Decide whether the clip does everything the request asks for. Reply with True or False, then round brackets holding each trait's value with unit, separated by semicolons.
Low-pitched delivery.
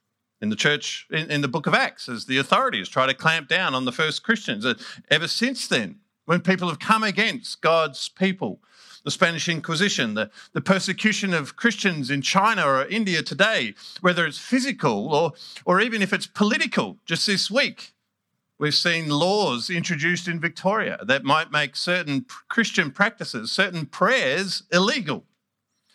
False (180 Hz)